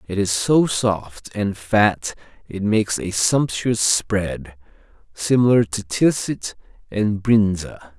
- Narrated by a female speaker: No, male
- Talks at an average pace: No, slow, 120 wpm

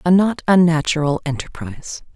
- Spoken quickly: No, slow, 110 wpm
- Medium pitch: Yes, medium, 165 Hz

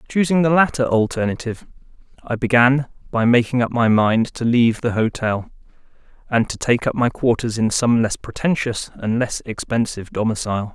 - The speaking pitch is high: No, low, 120 Hz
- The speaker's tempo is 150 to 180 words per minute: Yes, average, 160 wpm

